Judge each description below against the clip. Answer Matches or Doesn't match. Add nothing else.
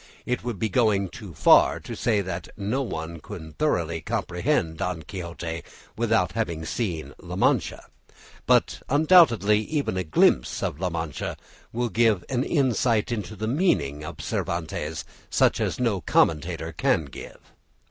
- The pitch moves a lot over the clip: Matches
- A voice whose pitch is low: Matches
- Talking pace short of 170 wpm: Matches